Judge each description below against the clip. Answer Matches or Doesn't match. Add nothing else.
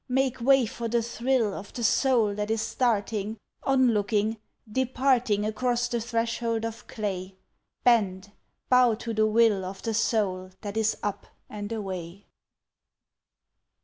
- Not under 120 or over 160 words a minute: Matches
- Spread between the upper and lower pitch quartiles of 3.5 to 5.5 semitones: Doesn't match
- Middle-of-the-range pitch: Doesn't match